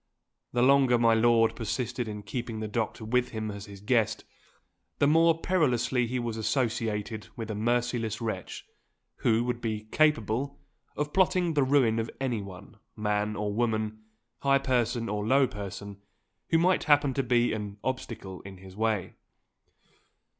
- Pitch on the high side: No, low, 115 Hz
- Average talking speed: Yes, average, 155 wpm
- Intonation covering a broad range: No, average, 3.4 semitones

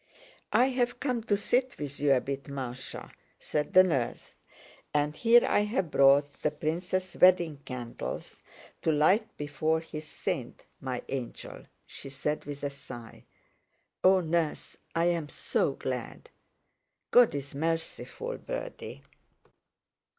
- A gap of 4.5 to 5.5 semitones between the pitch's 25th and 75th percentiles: Yes, average, 5.1 semitones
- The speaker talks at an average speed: No, slow, 120 wpm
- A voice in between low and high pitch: Yes, medium, 155 Hz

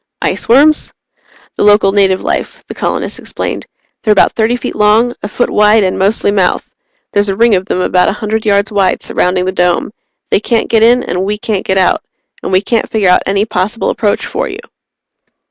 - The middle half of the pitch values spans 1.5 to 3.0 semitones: Yes, narrow, 2.6 semitones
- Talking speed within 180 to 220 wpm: Yes, average, 195 wpm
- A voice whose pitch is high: Yes, high, 205 Hz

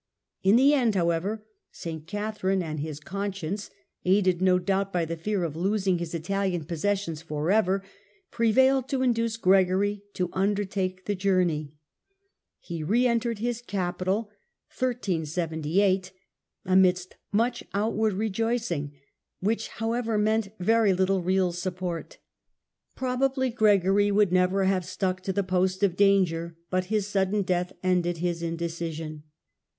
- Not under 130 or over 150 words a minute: Yes, slow, 135 wpm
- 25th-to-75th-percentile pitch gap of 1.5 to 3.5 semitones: Yes, average, 3.1 semitones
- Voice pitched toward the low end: No, high, 190 Hz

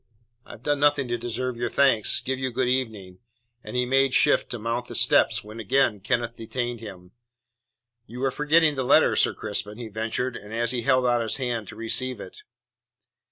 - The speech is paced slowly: No, average, 195 wpm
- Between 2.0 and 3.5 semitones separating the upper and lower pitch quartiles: Yes, average, 2.7 semitones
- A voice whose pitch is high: No, low, 120 Hz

